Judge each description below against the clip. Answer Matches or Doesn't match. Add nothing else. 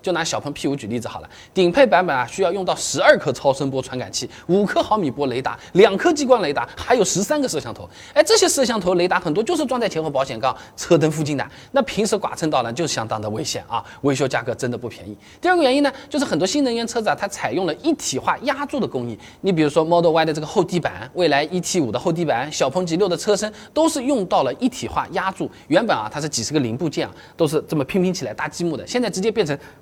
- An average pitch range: Doesn't match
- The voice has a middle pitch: Matches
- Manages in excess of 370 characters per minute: Matches